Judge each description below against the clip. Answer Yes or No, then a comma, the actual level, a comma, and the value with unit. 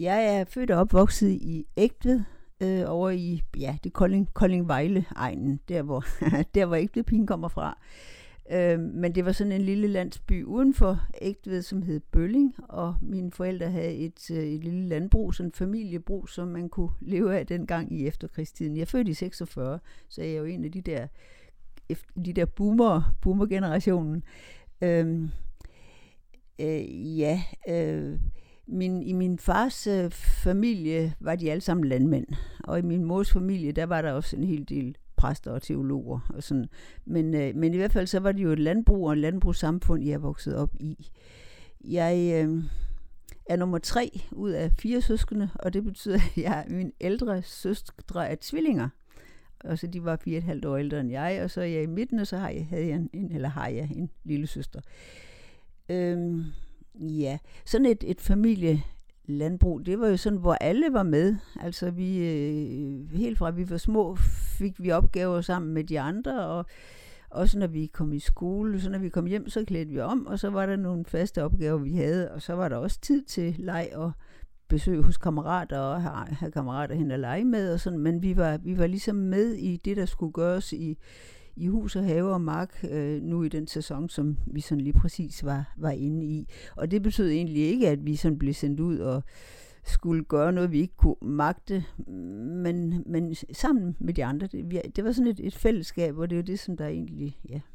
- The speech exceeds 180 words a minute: Yes, average, 200 wpm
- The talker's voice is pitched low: No, medium, 170 Hz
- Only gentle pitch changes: No, average, 3.6 semitones